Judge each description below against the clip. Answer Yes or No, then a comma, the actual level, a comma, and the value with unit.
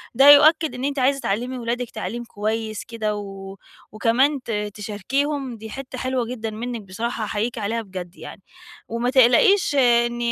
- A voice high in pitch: Yes, high, 235 Hz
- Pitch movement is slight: No, average, 3.3 semitones